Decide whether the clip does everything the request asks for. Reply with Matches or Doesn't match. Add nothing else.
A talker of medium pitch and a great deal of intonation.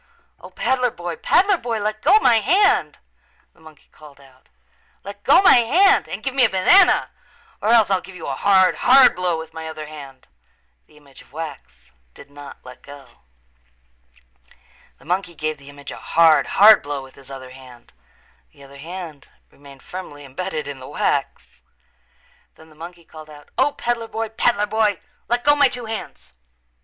Matches